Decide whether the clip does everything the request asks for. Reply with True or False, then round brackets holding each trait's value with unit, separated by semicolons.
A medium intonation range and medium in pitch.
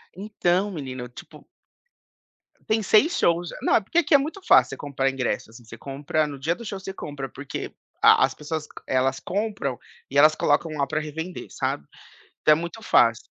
False (6.1 semitones; 155 Hz)